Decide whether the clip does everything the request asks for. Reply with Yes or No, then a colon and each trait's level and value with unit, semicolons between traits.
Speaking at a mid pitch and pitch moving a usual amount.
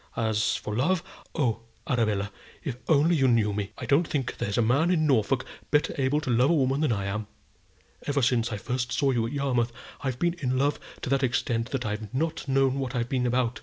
No: low, 130 Hz; average, 3.4 semitones